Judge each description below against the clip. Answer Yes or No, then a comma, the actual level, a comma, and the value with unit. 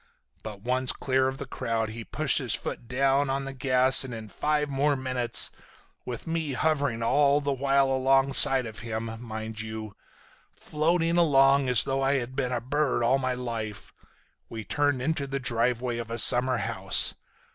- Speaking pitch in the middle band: No, low, 130 Hz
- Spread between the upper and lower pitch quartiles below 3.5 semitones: Yes, average, 2.9 semitones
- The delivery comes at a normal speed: Yes, average, 165 wpm